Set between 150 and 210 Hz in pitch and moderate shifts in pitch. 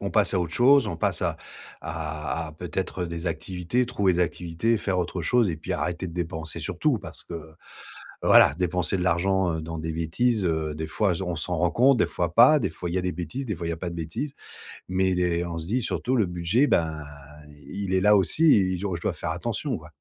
No: very low, 90 Hz; average, 3.2 semitones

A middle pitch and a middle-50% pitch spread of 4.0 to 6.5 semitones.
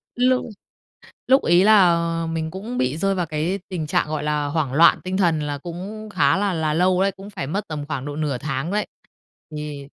Yes: medium, 165 Hz; average, 4.3 semitones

